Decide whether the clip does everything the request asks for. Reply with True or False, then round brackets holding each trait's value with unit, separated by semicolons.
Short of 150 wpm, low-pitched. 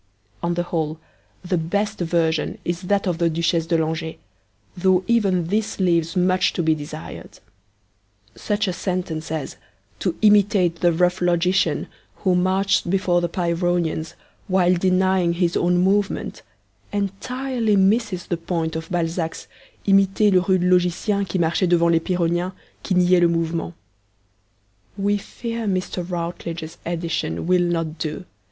False (140 wpm; 180 Hz)